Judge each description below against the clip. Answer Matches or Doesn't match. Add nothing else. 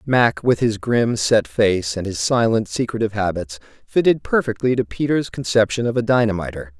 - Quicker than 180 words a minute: Doesn't match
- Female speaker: Doesn't match